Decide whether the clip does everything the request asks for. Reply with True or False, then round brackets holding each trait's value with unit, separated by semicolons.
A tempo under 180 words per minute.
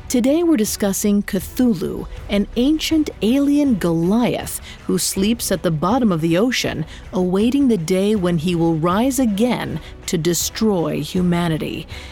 True (135 wpm)